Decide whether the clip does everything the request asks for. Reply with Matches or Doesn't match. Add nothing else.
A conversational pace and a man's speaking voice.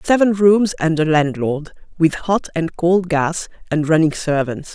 Doesn't match